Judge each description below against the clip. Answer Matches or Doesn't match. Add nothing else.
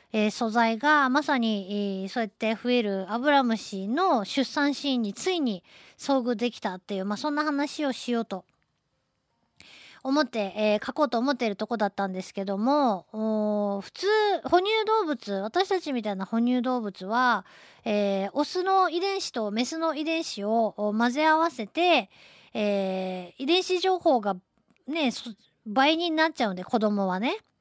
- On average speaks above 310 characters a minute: Doesn't match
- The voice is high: Matches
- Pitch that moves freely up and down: Matches